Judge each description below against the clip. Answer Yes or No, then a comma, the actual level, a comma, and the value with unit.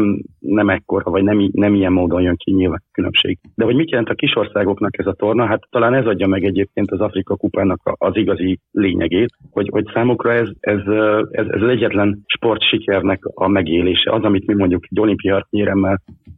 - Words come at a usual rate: No, fast, 195 wpm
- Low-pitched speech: Yes, low, 100 Hz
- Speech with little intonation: Yes, narrow, 1.6 semitones